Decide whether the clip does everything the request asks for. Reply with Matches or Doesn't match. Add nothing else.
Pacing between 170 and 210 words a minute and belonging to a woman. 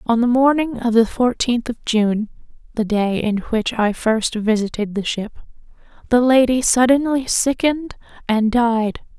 Doesn't match